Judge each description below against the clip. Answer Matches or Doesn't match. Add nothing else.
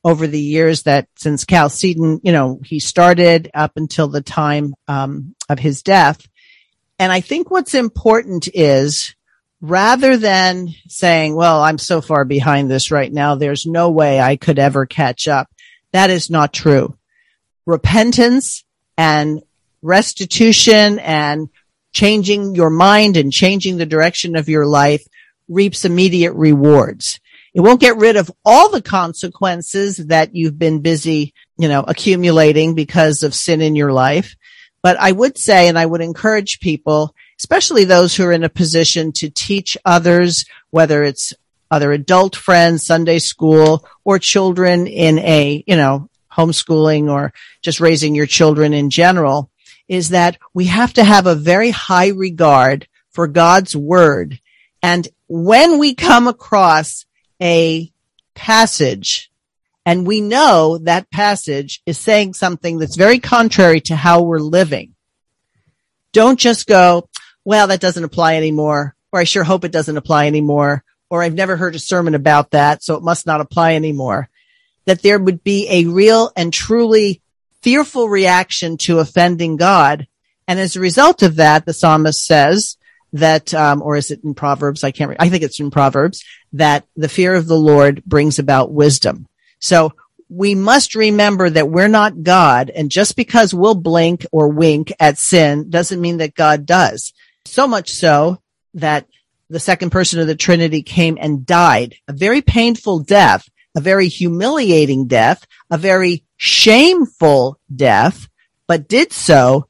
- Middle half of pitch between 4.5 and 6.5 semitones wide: Doesn't match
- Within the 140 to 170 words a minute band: Matches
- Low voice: Doesn't match